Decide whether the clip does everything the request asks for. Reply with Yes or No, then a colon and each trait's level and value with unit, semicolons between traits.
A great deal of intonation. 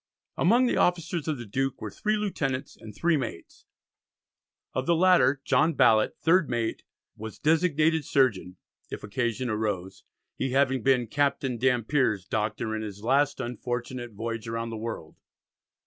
No: average, 4.8 semitones